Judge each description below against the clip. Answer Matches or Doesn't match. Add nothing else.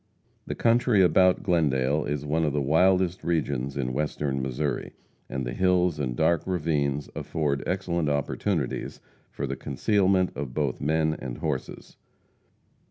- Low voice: Matches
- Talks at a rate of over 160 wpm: Doesn't match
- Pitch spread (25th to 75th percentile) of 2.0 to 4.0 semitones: Doesn't match